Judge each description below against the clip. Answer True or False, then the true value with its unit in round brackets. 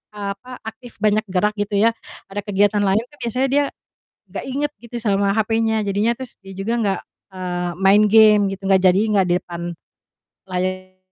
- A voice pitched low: False (205 Hz)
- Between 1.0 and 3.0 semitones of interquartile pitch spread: True (2.5 semitones)